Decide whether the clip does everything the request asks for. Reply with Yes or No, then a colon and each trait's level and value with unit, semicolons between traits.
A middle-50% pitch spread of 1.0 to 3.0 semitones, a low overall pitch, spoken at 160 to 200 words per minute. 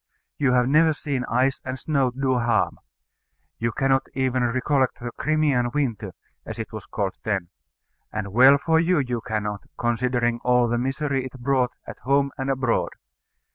Yes: narrow, 2.4 semitones; low, 130 Hz; average, 165 wpm